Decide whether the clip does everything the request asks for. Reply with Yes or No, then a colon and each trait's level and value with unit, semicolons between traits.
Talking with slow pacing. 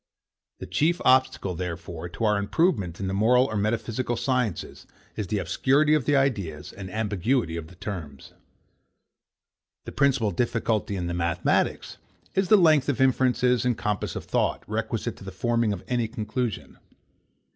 No: average, 155 wpm